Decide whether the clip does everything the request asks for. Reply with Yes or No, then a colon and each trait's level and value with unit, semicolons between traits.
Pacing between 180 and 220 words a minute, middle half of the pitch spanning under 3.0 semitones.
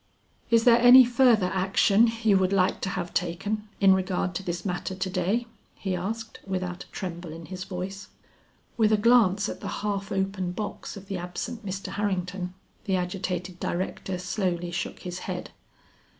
No: average, 170 wpm; narrow, 2.4 semitones